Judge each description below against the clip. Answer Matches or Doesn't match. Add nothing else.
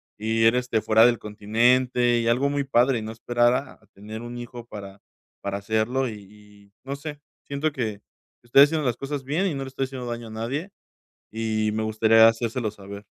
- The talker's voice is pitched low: Matches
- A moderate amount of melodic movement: Matches